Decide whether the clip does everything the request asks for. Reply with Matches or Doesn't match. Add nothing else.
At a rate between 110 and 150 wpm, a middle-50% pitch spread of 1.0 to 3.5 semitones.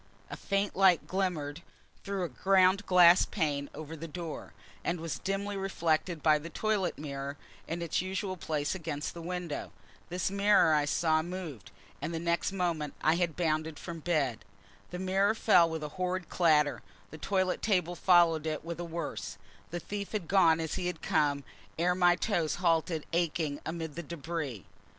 Doesn't match